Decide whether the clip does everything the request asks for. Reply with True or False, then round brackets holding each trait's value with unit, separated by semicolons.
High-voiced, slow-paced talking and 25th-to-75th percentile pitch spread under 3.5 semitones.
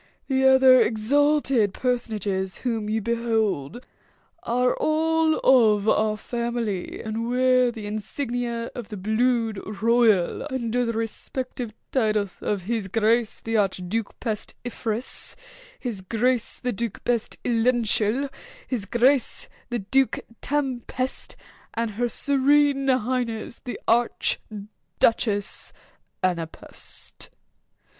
True (235 Hz; 105 wpm; 2.9 semitones)